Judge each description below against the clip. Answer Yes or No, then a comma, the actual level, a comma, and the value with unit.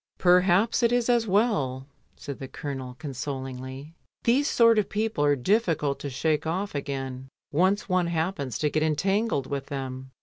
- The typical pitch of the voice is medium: Yes, medium, 155 Hz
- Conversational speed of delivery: Yes, average, 165 wpm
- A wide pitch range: Yes, wide, 6.8 semitones